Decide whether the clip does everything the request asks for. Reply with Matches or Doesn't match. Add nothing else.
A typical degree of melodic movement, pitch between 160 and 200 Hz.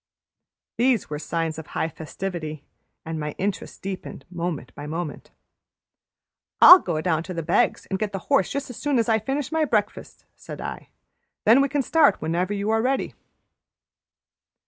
Doesn't match